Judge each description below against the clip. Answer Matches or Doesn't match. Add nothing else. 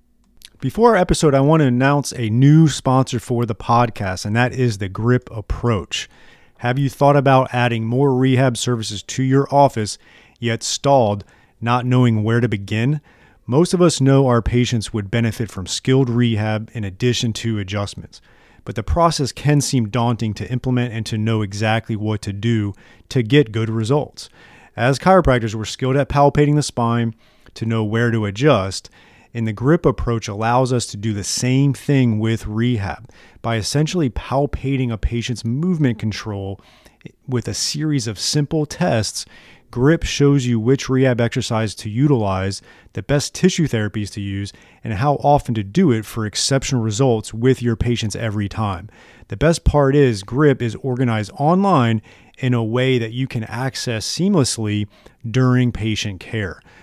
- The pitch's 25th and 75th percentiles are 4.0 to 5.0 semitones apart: Doesn't match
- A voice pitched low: Matches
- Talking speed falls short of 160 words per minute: Doesn't match